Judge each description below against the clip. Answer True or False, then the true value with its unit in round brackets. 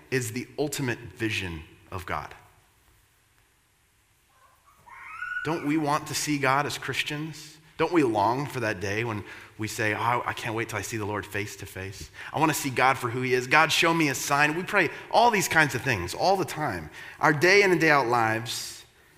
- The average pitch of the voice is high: False (125 Hz)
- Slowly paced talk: False (205 wpm)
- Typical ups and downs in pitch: False (5.7 semitones)